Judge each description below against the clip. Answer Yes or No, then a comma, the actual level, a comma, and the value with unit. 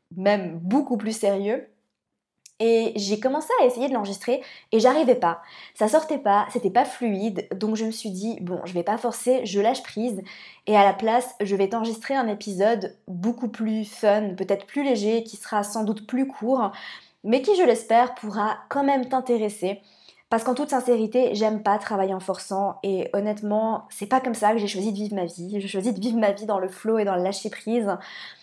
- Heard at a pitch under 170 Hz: No, high, 215 Hz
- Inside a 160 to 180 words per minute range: No, average, 205 wpm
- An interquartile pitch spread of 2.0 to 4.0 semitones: Yes, average, 3.2 semitones